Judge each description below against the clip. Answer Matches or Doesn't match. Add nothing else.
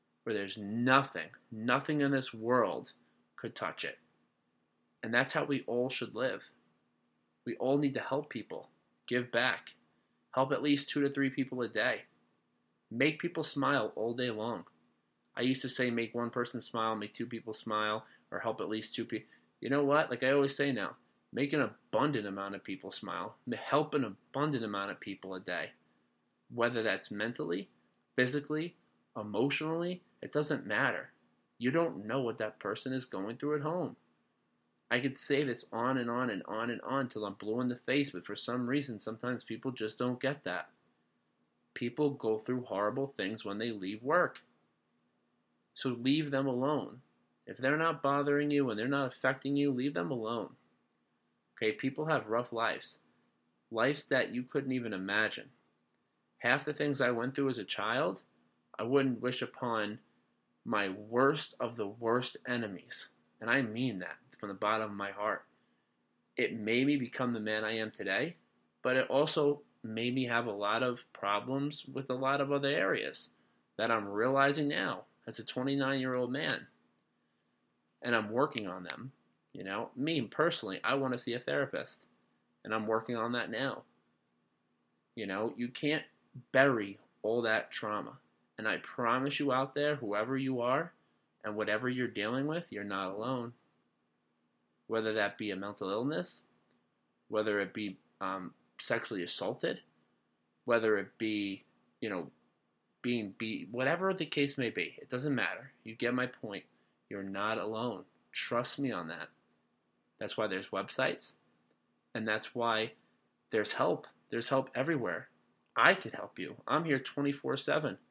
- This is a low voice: Matches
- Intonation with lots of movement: Matches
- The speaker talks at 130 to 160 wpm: Doesn't match